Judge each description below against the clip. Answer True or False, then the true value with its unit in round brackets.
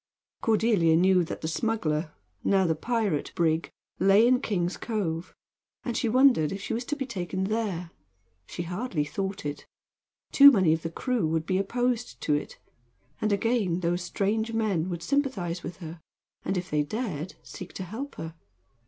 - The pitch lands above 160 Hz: True (190 Hz)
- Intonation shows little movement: False (5.3 semitones)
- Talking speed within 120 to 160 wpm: False (170 wpm)